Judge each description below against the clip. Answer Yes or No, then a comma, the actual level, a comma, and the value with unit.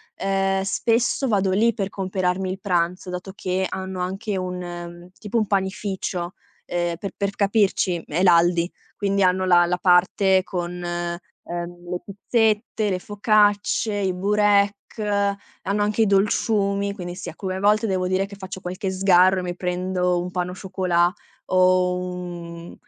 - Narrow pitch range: Yes, narrow, 1.9 semitones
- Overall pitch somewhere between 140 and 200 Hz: Yes, high, 190 Hz